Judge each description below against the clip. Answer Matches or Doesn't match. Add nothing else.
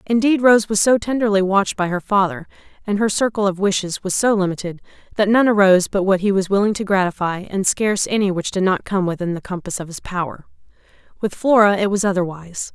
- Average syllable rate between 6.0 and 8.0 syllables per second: Matches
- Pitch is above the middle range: Matches